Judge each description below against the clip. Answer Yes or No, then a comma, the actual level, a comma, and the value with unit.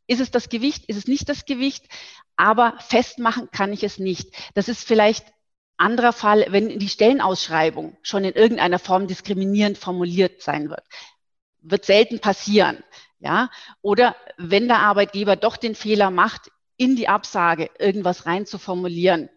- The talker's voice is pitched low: No, high, 205 Hz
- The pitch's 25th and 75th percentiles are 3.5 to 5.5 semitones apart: Yes, average, 3.9 semitones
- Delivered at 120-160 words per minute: Yes, average, 150 wpm